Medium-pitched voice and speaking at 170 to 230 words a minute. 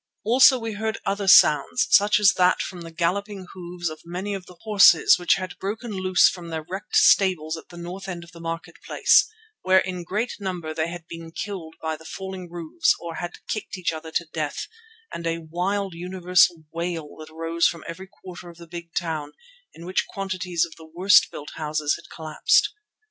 Yes: medium, 175 Hz; average, 195 wpm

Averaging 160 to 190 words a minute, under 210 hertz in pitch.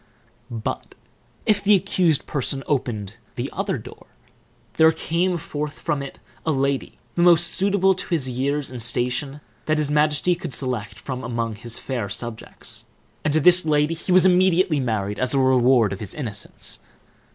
Yes: average, 165 wpm; medium, 140 Hz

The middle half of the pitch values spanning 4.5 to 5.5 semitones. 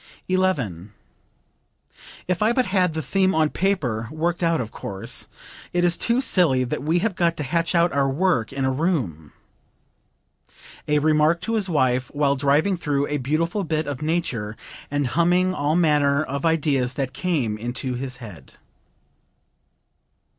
Yes: average, 4.9 semitones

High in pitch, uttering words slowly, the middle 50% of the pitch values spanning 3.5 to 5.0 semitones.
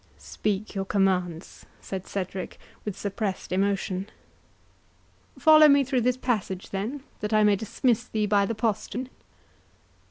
Yes: high, 210 Hz; slow, 130 wpm; average, 3.8 semitones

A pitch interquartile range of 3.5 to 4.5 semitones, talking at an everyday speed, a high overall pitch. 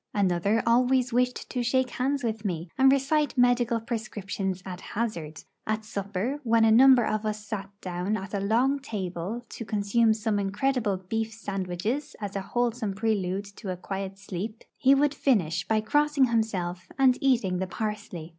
Yes: average, 4.1 semitones; average, 165 wpm; high, 215 Hz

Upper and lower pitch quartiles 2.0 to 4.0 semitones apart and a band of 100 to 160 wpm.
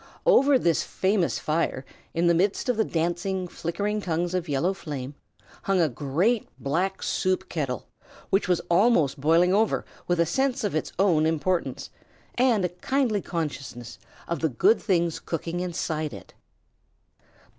Yes: average, 3.7 semitones; average, 155 wpm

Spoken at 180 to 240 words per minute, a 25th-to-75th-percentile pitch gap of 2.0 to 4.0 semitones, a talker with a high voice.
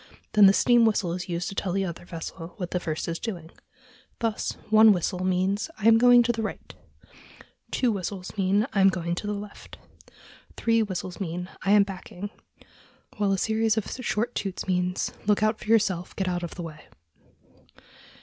Yes: average, 190 wpm; average, 3.3 semitones; high, 195 Hz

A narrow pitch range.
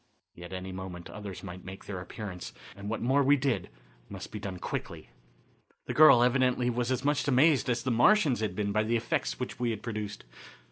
No: average, 4.9 semitones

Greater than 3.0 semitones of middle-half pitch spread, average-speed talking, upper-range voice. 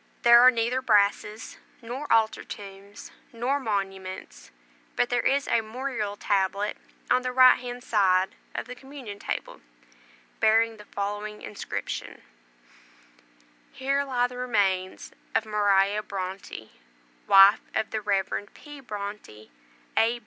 No: average, 3.6 semitones; slow, 125 wpm; high, 215 Hz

